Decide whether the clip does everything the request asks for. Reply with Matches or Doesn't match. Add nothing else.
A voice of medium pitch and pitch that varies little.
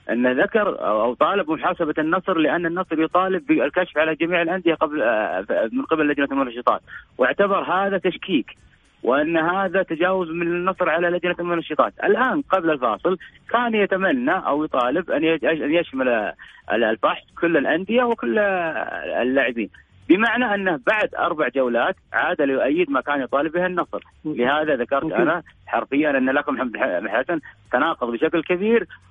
Doesn't match